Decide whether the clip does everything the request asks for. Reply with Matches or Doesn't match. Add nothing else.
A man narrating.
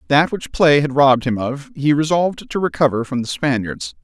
Matches